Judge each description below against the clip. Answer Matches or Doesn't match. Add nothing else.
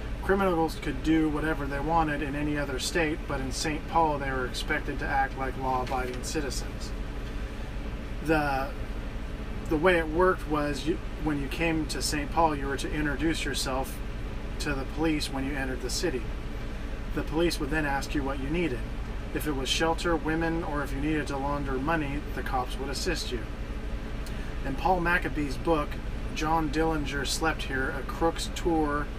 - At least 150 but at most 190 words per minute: Matches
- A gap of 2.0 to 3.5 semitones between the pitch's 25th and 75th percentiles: Matches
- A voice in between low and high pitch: Matches